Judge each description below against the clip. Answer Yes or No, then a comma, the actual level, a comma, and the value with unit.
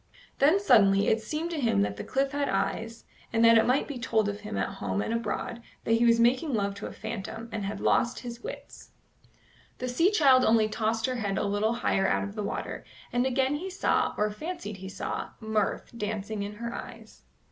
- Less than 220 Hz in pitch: No, high, 230 Hz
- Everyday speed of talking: No, fast, 215 wpm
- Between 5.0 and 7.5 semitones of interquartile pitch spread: No, average, 3.5 semitones